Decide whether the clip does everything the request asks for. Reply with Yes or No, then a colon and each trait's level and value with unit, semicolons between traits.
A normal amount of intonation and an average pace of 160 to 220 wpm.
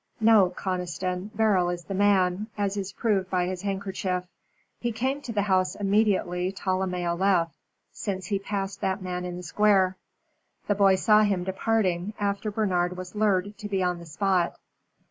No: narrow, 2.2 semitones; average, 165 wpm